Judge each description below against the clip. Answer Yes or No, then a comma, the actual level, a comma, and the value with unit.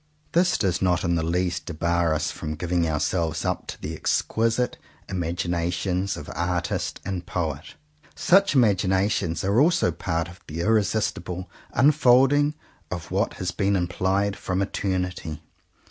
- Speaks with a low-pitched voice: Yes, very low, 90 Hz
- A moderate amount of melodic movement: Yes, average, 3.1 semitones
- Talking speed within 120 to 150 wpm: Yes, slow, 135 wpm